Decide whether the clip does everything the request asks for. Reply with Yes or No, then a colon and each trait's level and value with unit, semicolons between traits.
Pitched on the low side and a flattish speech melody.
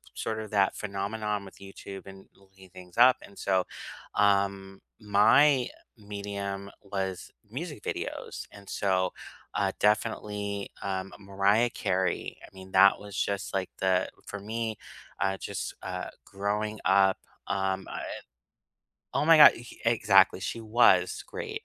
Yes: low, 100 Hz; narrow, 1.7 semitones